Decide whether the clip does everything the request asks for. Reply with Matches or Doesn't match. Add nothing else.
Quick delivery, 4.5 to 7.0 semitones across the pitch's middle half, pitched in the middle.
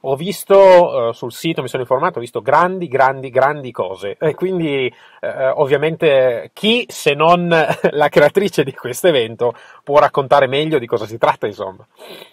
Doesn't match